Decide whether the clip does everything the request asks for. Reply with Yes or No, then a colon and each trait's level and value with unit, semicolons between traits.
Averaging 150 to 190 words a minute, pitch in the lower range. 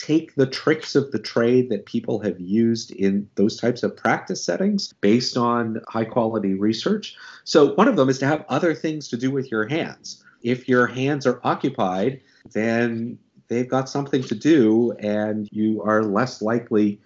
Yes: average, 180 wpm; low, 120 Hz